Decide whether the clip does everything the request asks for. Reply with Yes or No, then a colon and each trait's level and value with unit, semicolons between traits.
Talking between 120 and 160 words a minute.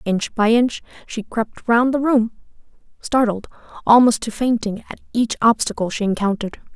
Yes: average, 150 wpm